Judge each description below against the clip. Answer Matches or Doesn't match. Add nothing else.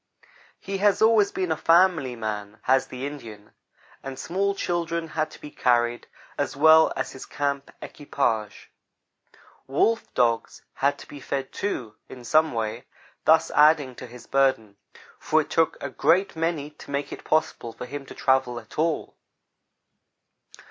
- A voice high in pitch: Doesn't match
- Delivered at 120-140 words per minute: Doesn't match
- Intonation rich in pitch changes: Doesn't match